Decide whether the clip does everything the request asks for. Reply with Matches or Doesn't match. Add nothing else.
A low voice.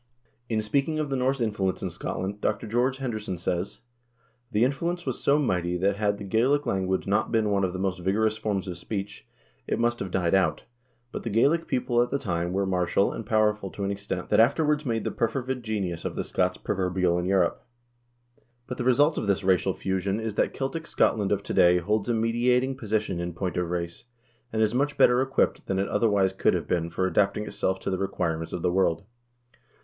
Matches